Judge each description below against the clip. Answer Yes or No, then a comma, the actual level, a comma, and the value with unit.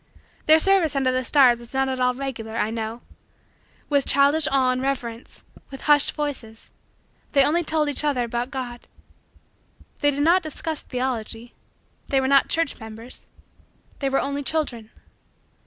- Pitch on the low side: No, very high, 270 Hz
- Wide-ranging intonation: No, average, 3.2 semitones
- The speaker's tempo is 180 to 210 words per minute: No, average, 155 wpm